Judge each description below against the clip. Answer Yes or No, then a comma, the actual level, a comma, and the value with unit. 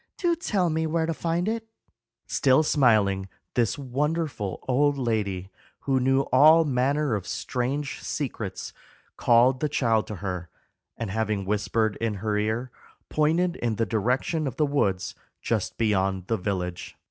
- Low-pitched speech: Yes, low, 125 Hz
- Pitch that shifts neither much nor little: No, wide, 6.0 semitones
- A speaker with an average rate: Yes, average, 145 wpm